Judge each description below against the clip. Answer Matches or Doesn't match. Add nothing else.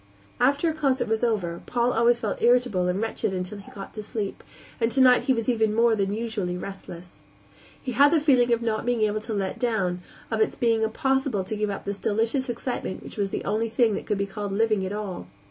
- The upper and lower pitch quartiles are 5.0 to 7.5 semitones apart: Doesn't match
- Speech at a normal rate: Doesn't match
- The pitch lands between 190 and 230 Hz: Matches